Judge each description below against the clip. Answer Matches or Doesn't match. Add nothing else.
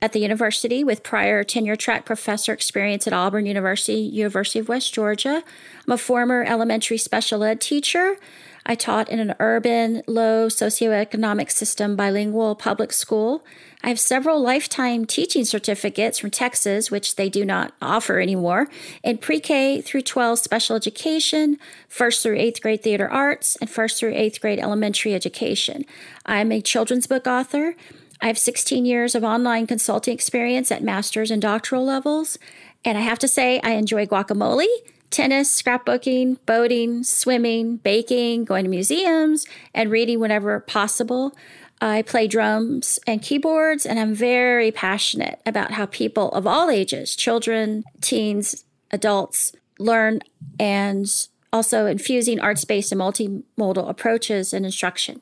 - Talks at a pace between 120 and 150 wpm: Matches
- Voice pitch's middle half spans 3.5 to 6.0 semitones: Doesn't match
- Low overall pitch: Doesn't match